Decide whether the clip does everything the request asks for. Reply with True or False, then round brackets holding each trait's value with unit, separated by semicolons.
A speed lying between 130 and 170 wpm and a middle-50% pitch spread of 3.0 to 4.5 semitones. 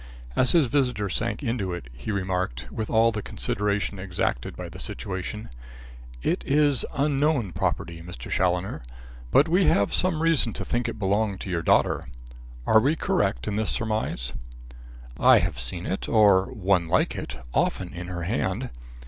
False (165 wpm; 5.0 semitones)